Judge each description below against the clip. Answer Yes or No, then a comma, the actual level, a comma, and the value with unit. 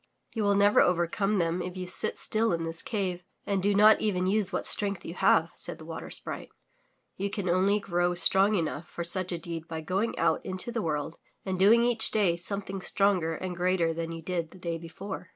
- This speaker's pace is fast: Yes, fast, 215 wpm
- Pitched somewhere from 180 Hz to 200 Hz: Yes, medium, 185 Hz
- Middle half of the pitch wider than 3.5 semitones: No, average, 3.0 semitones